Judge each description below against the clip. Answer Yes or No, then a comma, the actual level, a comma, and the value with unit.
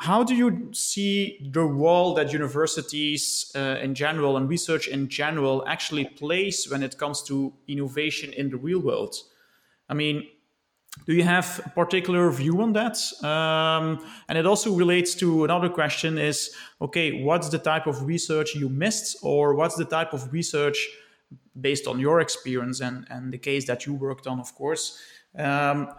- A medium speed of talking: Yes, average, 170 wpm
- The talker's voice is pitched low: No, medium, 155 Hz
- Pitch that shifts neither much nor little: Yes, average, 3.7 semitones